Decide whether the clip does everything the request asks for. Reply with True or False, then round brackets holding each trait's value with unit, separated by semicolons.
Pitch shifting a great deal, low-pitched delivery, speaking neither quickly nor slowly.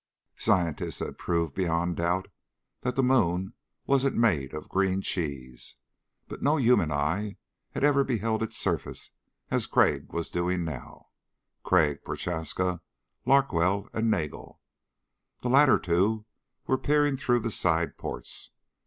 False (6.4 semitones; 95 Hz; 130 wpm)